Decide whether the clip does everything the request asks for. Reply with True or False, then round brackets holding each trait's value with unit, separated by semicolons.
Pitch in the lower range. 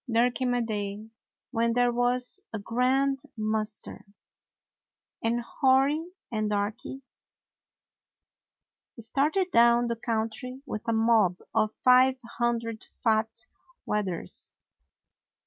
False (235 Hz)